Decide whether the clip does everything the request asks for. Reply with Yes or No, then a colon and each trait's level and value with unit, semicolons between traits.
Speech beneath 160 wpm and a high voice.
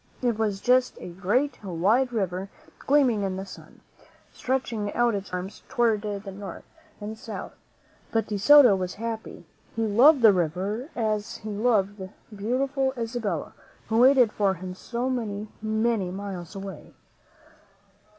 Yes: average, 150 wpm; high, 215 Hz